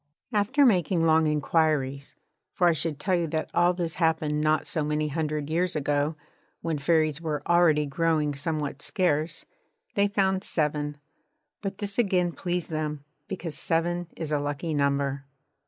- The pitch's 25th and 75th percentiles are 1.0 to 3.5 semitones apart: Yes, average, 2.7 semitones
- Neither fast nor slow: Yes, average, 155 wpm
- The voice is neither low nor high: Yes, medium, 160 Hz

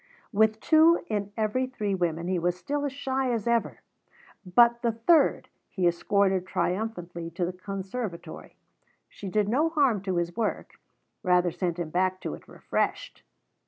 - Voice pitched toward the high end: Yes, high, 200 Hz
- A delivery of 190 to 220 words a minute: No, average, 160 wpm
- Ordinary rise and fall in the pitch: Yes, average, 4.8 semitones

